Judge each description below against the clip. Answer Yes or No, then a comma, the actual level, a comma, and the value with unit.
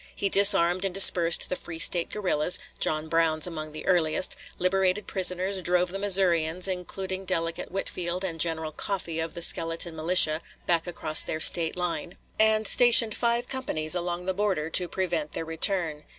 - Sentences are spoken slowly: No, average, 165 wpm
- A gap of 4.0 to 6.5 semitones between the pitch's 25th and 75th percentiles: No, average, 2.7 semitones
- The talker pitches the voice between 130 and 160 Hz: No, medium, 175 Hz